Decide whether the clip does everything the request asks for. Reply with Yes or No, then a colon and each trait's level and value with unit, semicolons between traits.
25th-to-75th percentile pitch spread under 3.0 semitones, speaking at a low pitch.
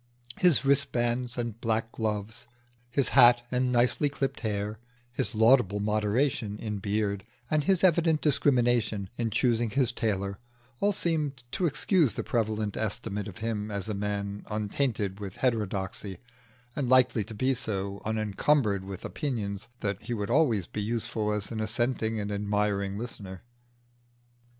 No: average, 3.6 semitones; low, 110 Hz